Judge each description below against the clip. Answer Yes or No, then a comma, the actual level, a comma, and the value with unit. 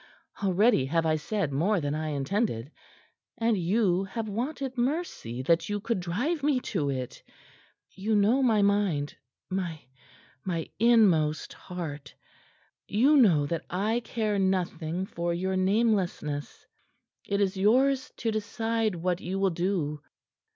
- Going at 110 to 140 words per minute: Yes, slow, 135 wpm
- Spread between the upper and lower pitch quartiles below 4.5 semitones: No, average, 5.2 semitones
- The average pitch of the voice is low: No, high, 190 Hz